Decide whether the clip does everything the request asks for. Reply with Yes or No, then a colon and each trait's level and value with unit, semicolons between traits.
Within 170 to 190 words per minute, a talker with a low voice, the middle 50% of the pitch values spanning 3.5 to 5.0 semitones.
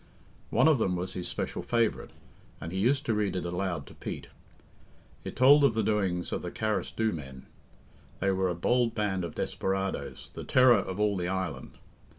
Yes: average, 185 wpm; very low, 95 Hz; average, 3.9 semitones